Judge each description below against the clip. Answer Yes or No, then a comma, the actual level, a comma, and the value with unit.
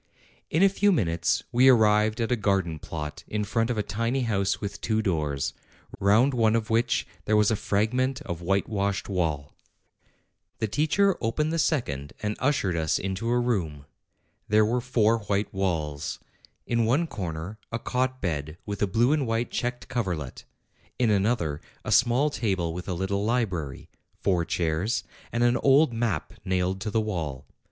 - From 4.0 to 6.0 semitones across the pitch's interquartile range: Yes, average, 5.1 semitones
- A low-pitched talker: Yes, low, 105 Hz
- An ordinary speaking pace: Yes, average, 170 wpm